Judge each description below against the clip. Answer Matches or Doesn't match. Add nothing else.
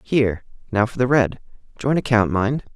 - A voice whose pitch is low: Matches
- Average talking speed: Matches